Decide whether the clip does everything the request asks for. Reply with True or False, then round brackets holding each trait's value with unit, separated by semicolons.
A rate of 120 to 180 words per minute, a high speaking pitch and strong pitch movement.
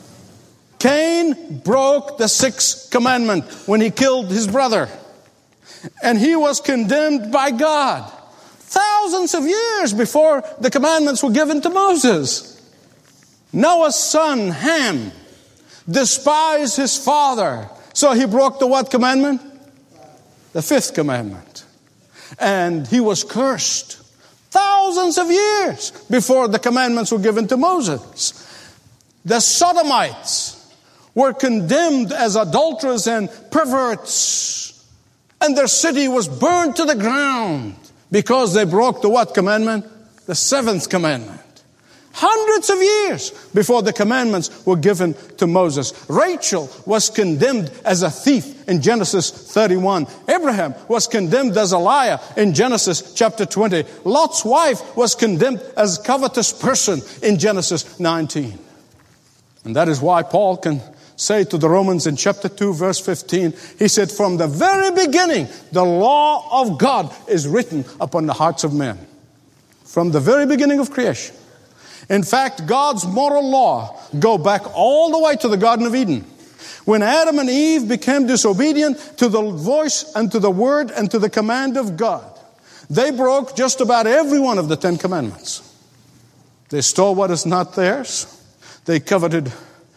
True (140 wpm; 230 Hz; 7.1 semitones)